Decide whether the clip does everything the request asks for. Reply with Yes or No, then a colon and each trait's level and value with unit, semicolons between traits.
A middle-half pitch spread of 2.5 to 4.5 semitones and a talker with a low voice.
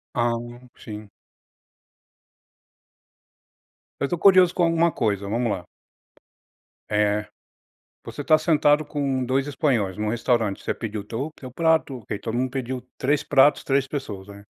No: wide, 5.4 semitones; low, 130 Hz